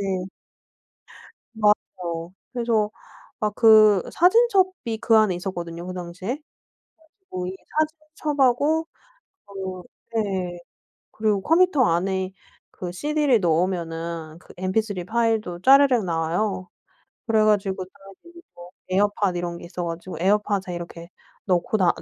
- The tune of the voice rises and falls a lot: No, average, 4.1 semitones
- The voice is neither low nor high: No, high, 195 Hz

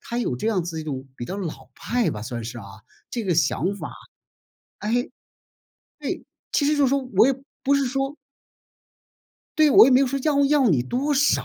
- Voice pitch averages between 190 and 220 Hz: No, high, 240 Hz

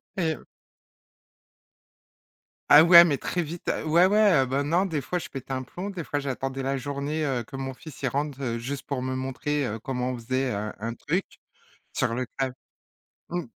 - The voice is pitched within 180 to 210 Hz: No, medium, 140 Hz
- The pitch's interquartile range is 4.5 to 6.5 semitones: No, average, 3.6 semitones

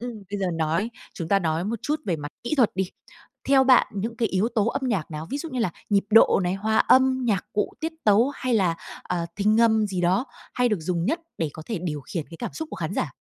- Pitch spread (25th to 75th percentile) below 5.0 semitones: No, wide, 5.4 semitones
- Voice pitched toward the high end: Yes, high, 205 Hz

